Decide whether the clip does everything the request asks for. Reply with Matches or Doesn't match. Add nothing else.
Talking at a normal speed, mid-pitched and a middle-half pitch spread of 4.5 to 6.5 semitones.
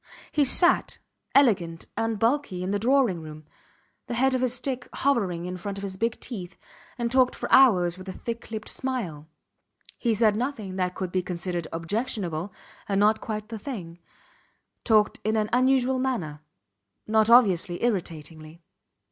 Doesn't match